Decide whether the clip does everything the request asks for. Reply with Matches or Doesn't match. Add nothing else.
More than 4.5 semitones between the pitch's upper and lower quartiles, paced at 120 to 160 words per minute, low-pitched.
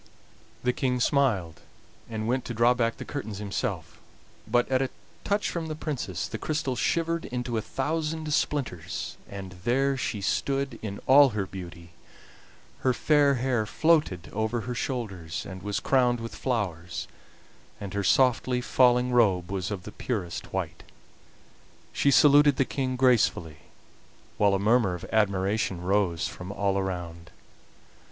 Matches